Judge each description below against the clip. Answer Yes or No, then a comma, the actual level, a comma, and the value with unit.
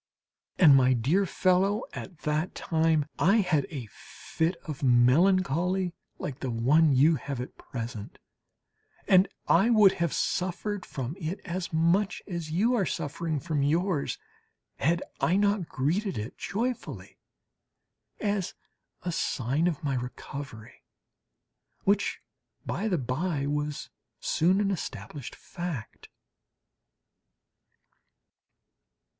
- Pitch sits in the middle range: Yes, medium, 165 Hz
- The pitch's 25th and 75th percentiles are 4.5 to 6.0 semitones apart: Yes, average, 5.1 semitones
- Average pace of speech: No, slow, 115 wpm